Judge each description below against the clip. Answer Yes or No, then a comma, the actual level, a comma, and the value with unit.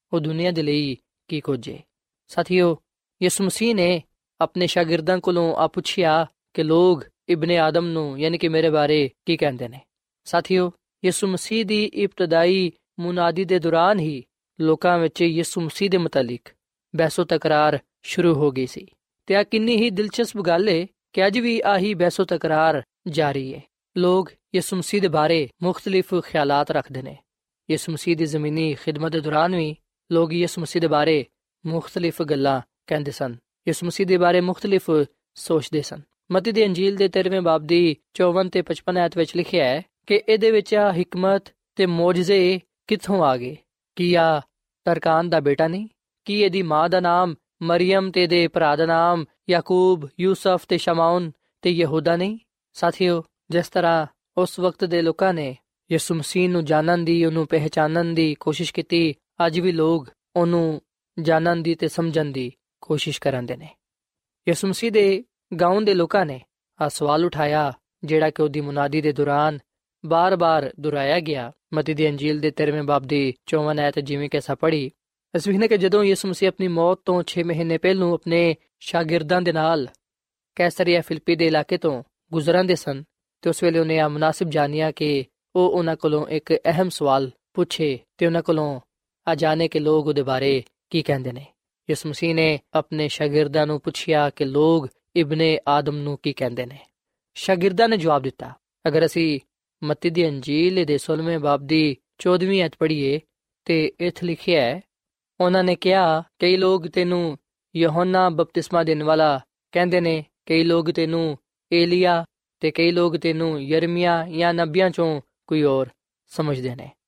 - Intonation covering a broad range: No, average, 2.8 semitones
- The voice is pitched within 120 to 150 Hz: No, medium, 165 Hz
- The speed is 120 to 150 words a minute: No, average, 160 wpm